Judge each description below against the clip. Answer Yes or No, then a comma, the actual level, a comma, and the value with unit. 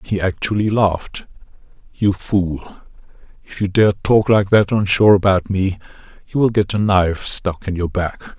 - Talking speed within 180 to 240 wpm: No, average, 170 wpm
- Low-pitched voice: Yes, very low, 95 Hz